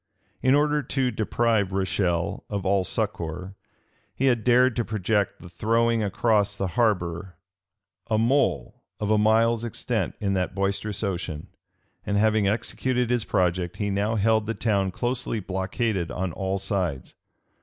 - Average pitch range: Yes, average, 3.4 semitones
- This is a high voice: No, low, 105 Hz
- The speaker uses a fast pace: No, average, 145 wpm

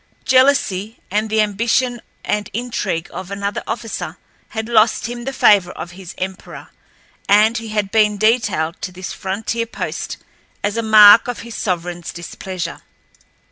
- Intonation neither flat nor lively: Yes, average, 3.3 semitones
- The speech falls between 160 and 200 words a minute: No, average, 145 wpm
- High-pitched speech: Yes, high, 210 Hz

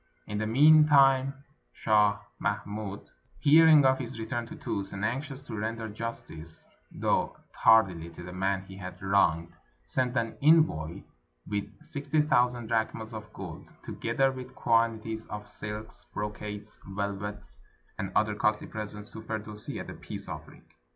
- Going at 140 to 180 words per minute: Yes, average, 150 wpm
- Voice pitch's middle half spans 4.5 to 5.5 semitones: No, average, 3.6 semitones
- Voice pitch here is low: Yes, low, 110 Hz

